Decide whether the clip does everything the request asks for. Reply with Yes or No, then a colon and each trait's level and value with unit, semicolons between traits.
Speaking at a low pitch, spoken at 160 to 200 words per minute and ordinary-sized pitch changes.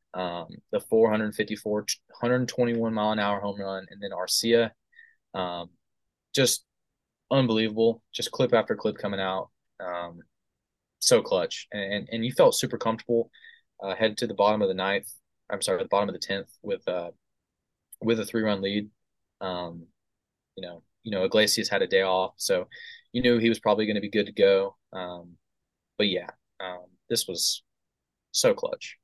Yes: low, 110 Hz; average, 175 wpm; average, 3.9 semitones